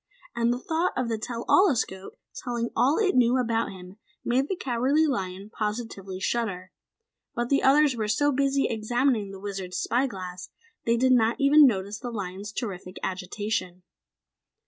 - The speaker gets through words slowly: No, average, 165 wpm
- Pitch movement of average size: Yes, average, 4.8 semitones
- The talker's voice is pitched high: Yes, high, 230 Hz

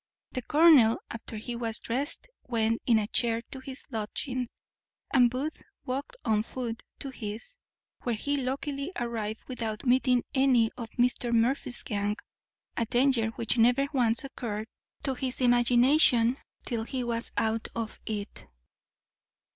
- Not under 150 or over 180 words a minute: No, average, 140 wpm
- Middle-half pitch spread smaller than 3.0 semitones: Yes, narrow, 2.6 semitones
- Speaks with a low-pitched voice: No, high, 240 Hz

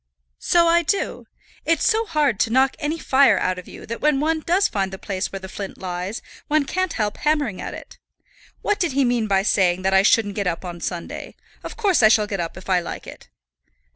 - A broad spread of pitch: Yes, wide, 8.2 semitones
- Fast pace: Yes, fast, 230 wpm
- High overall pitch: Yes, high, 225 Hz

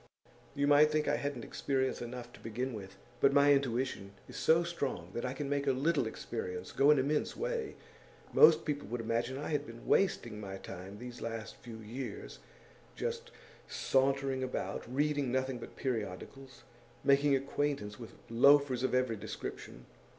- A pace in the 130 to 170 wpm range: Yes, average, 165 wpm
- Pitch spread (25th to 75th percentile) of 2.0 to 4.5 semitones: Yes, average, 3.7 semitones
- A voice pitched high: No, low, 130 Hz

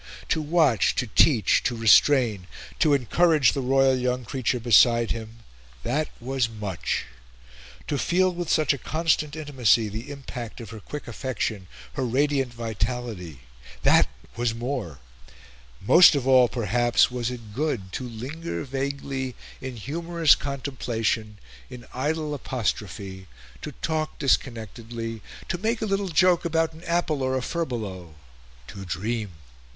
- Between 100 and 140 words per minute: Yes, slow, 135 wpm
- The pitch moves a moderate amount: Yes, average, 4.6 semitones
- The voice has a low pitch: Yes, low, 125 Hz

